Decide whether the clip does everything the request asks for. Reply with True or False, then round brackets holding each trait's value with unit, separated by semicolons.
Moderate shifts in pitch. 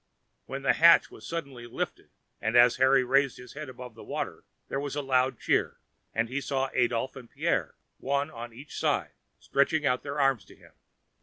False (2.2 semitones)